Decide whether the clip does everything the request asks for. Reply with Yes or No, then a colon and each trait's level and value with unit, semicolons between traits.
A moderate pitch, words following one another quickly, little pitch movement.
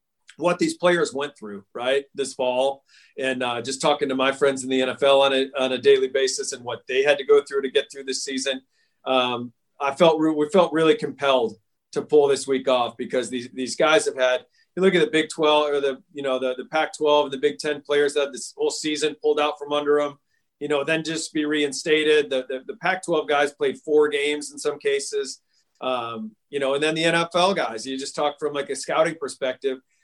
No: medium, 145 Hz; fast, 230 wpm; average, 3.2 semitones